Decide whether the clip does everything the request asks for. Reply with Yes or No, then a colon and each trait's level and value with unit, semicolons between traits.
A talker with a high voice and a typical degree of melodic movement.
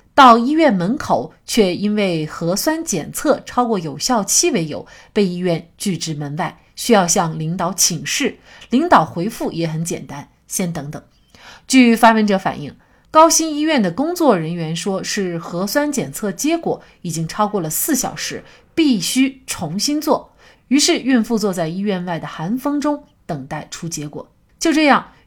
No: high, 200 Hz; wide, 7.7 semitones